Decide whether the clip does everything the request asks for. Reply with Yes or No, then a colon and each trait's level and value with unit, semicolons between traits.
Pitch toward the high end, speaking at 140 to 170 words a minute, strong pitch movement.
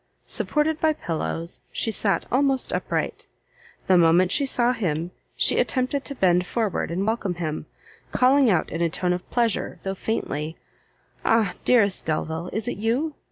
Yes: high, 200 Hz; average, 160 wpm; wide, 6.5 semitones